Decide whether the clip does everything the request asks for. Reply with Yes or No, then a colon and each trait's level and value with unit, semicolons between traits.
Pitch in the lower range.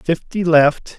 No: medium, 160 Hz